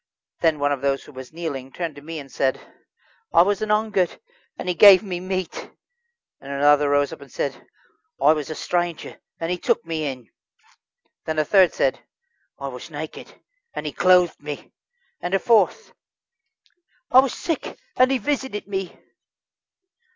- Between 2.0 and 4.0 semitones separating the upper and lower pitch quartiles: No, average, 5.2 semitones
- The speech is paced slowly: No, average, 170 wpm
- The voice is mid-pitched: Yes, medium, 170 Hz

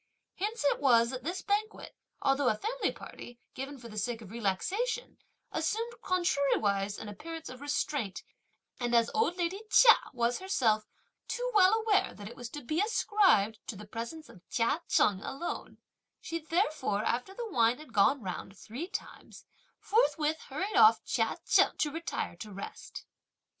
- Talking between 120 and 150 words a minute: No, average, 165 wpm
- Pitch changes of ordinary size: No, wide, 8.5 semitones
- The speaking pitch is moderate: No, very high, 285 Hz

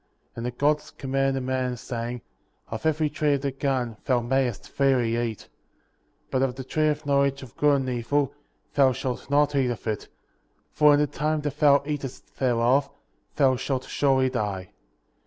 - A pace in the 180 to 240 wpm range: Yes, average, 185 wpm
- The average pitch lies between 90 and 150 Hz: Yes, low, 135 Hz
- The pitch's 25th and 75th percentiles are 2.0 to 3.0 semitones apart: Yes, narrow, 2.6 semitones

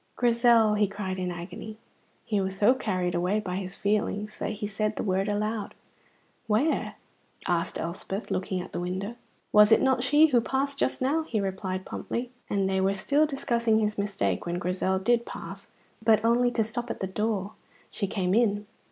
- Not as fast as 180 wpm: No, average, 185 wpm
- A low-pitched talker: No, high, 210 Hz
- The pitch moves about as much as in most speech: Yes, average, 3.6 semitones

